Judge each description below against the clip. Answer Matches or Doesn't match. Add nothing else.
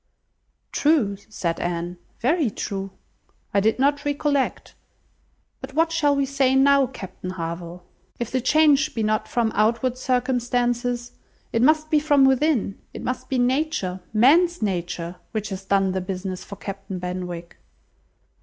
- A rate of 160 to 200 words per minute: Doesn't match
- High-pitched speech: Matches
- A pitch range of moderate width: Doesn't match